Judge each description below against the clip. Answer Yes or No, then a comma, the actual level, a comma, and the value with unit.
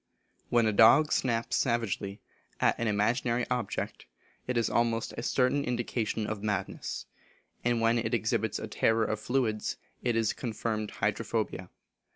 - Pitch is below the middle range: Yes, low, 115 Hz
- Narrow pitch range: Yes, narrow, 1.8 semitones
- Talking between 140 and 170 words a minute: Yes, average, 145 wpm